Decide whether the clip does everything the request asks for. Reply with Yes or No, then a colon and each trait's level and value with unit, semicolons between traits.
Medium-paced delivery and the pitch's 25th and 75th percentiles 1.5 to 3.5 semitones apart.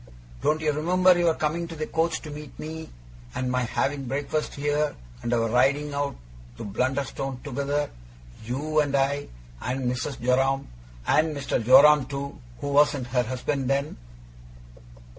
Yes: average, 150 wpm; narrow, 2.6 semitones